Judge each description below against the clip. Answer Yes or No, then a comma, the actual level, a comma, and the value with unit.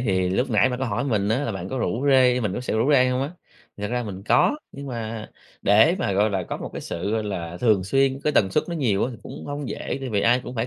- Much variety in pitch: No, average, 4.6 semitones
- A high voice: No, low, 115 Hz